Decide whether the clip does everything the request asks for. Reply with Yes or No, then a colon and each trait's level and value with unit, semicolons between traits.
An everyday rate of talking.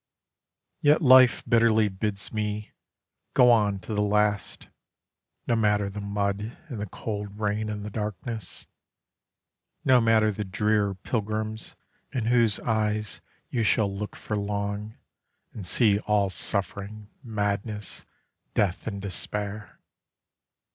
No: slow, 120 wpm